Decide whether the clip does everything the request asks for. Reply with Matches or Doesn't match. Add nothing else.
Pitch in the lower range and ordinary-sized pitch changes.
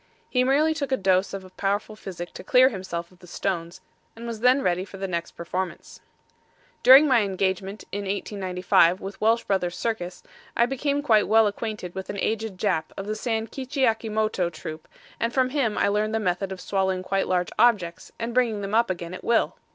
Doesn't match